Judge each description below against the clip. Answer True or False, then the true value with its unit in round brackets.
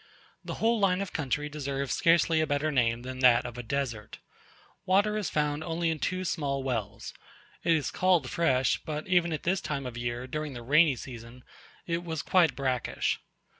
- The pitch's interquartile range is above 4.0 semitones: True (4.8 semitones)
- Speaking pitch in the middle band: True (150 Hz)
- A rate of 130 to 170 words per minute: False (190 wpm)